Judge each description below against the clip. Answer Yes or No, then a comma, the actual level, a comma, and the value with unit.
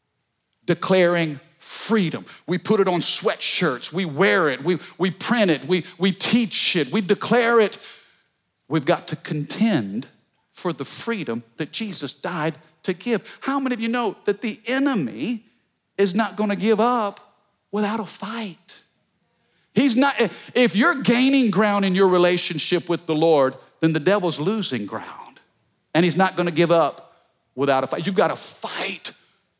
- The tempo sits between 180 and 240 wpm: No, average, 165 wpm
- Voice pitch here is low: No, high, 190 Hz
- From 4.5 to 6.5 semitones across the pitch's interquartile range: Yes, average, 5.1 semitones